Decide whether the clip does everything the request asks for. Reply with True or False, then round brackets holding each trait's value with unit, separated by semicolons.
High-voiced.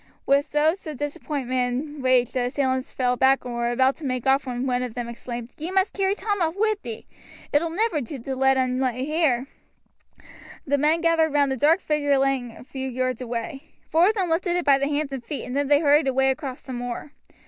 True (270 Hz)